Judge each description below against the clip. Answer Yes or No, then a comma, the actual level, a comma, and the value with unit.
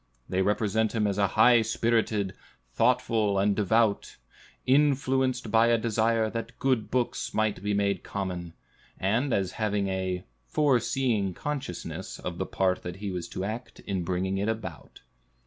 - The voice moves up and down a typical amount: Yes, average, 3.4 semitones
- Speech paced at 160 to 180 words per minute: No, average, 145 wpm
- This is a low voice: Yes, low, 105 Hz